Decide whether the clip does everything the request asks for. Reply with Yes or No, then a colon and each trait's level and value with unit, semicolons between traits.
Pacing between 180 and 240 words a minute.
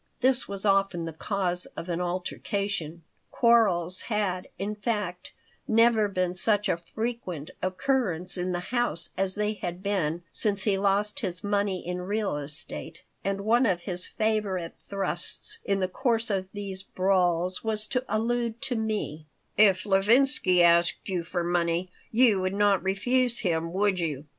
No: average, 155 wpm